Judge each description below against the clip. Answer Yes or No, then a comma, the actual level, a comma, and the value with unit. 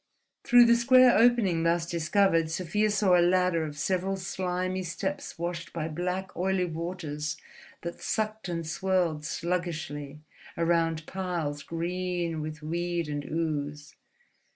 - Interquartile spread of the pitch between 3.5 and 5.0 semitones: No, narrow, 2.6 semitones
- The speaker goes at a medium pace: No, slow, 130 wpm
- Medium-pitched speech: Yes, medium, 175 Hz